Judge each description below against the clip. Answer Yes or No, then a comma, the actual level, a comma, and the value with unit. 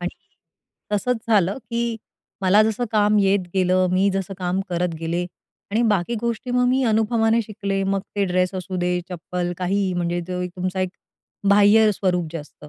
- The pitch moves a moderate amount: Yes, average, 3.1 semitones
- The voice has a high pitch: Yes, high, 195 Hz